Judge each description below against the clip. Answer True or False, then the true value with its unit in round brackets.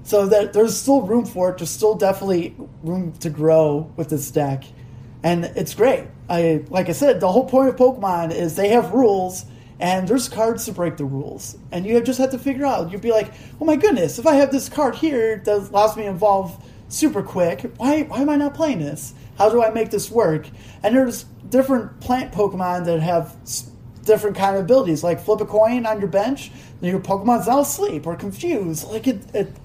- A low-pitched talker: False (195 Hz)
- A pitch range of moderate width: False (6.5 semitones)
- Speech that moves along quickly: True (215 wpm)